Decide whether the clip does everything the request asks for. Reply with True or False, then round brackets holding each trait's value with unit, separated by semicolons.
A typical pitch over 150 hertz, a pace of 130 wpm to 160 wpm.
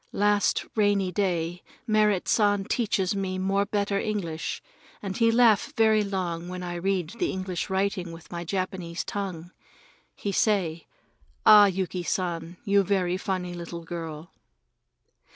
True (190 Hz; 135 wpm)